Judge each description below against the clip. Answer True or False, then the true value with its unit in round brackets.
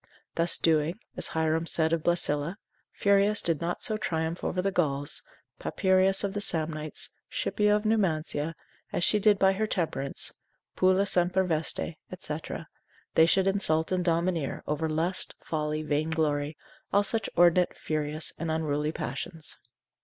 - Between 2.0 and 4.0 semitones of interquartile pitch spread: True (3.5 semitones)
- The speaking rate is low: False (145 wpm)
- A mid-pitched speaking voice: True (165 Hz)